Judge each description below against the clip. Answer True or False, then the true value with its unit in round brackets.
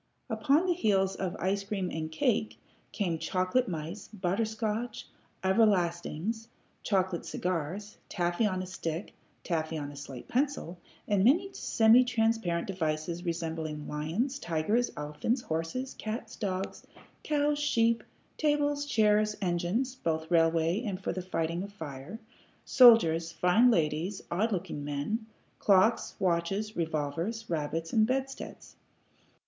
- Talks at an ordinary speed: False (125 wpm)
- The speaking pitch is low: False (190 Hz)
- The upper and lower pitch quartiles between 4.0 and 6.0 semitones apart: True (5.4 semitones)